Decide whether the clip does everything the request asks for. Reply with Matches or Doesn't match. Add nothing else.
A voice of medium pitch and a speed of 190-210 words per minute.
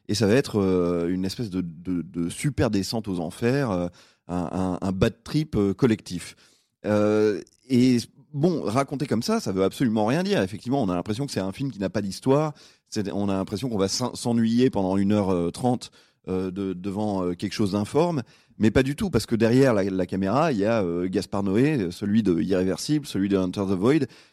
Doesn't match